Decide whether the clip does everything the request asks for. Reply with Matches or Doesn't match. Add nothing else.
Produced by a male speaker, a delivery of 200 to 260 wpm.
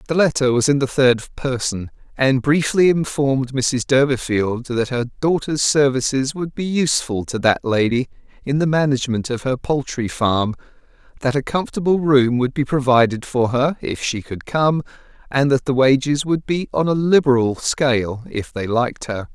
Doesn't match